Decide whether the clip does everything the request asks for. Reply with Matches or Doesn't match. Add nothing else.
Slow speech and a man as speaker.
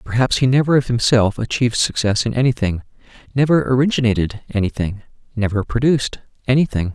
Matches